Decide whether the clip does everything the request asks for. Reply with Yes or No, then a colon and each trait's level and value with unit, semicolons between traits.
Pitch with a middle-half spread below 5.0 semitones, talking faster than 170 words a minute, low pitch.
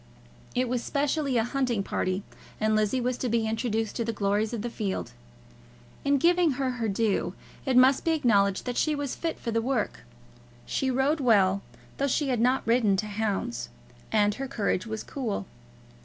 No: average, 3.9 semitones; average, 185 wpm; high, 235 Hz